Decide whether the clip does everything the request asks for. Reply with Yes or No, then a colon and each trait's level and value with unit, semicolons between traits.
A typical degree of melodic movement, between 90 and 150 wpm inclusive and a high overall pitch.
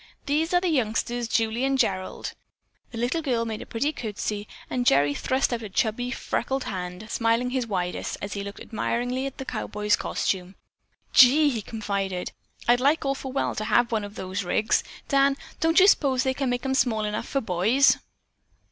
No: average, 4.3 semitones; average, 185 wpm; high, 235 Hz